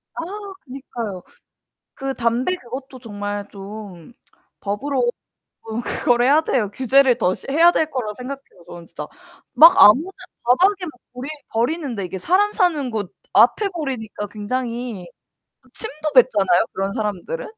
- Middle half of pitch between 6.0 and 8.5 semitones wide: No, wide, 5.5 semitones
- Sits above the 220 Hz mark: Yes, high, 245 Hz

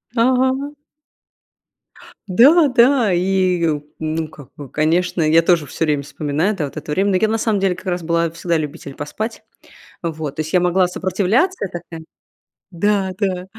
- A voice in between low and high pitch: Yes, medium, 180 Hz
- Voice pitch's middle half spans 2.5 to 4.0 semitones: No, average, 4.5 semitones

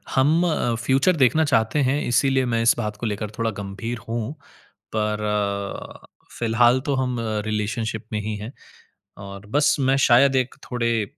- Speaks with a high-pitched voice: No, low, 115 Hz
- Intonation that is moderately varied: Yes, average, 3.7 semitones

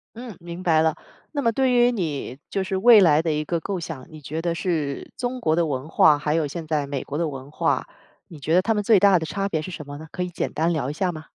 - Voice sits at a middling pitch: Yes, medium, 165 Hz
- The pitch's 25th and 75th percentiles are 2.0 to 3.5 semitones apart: No, average, 4.0 semitones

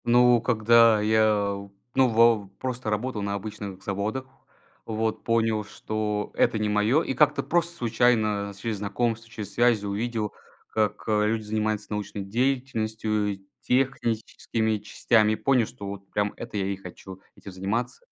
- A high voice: No, low, 110 Hz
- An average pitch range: No, narrow, 2.3 semitones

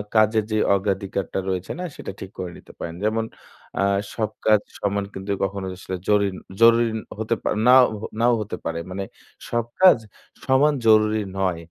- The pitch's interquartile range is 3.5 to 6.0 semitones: No, average, 2.8 semitones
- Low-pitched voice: Yes, low, 105 Hz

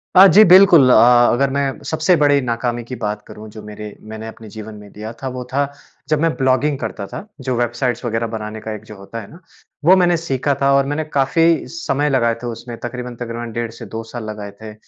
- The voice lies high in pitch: No, low, 120 Hz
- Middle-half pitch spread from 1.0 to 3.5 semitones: No, average, 4.2 semitones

